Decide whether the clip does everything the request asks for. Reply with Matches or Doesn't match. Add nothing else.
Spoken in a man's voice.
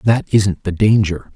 Matches